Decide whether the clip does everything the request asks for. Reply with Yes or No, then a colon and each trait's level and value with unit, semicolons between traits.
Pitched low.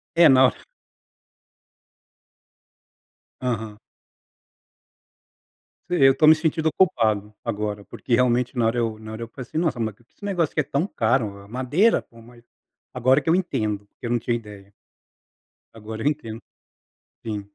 Yes: low, 120 Hz